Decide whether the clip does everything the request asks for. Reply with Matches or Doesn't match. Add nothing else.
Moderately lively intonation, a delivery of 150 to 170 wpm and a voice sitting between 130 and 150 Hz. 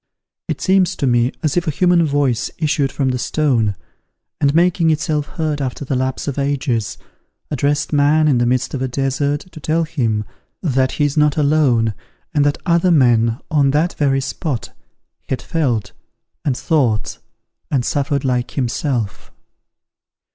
Matches